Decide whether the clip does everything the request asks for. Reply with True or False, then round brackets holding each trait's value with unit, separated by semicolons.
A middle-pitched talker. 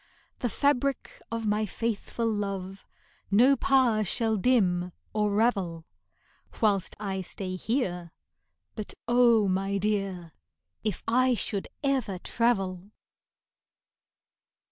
False (210 Hz)